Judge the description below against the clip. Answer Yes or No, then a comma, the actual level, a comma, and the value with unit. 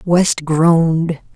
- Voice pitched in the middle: Yes, medium, 165 Hz